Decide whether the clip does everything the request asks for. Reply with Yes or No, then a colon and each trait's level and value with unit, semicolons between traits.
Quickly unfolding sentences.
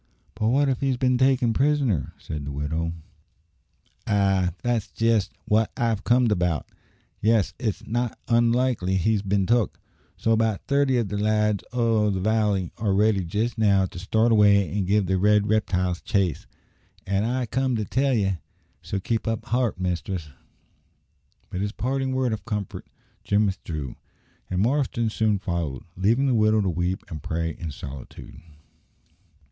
No: average, 160 wpm